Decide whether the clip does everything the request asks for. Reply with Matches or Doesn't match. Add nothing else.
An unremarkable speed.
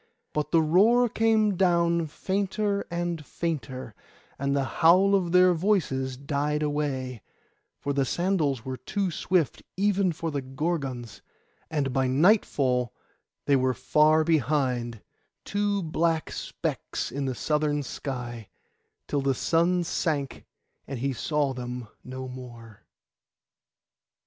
Doesn't match